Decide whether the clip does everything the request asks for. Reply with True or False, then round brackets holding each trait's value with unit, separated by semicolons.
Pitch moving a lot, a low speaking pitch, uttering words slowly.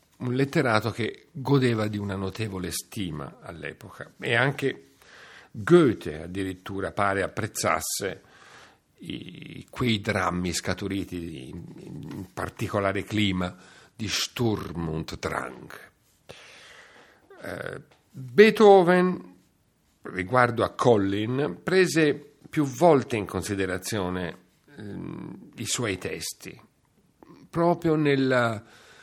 True (6.5 semitones; 110 Hz; 90 wpm)